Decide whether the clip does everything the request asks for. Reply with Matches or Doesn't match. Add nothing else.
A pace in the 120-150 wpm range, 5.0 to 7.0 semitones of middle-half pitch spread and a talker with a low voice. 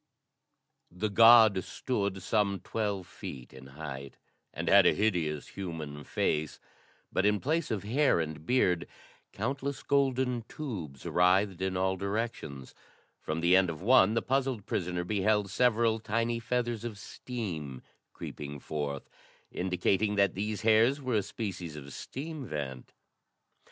Matches